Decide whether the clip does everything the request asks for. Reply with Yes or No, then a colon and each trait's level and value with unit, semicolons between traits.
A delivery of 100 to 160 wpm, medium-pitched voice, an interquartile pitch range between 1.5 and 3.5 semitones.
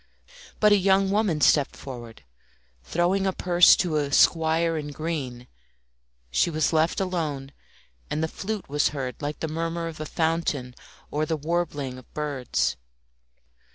Yes: average, 150 wpm; medium, 160 Hz; average, 3.2 semitones